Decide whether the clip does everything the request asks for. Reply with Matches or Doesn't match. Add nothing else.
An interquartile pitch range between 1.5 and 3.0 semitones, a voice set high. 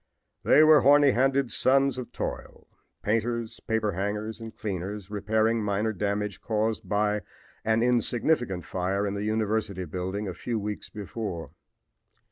Doesn't match